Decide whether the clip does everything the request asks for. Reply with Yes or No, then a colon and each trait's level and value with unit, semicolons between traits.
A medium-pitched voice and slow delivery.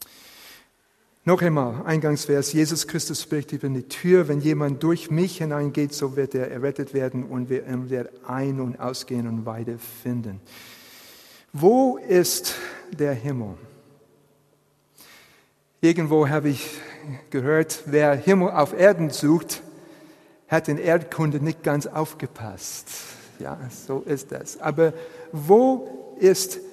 Yes: medium, 145 Hz; slow, 120 wpm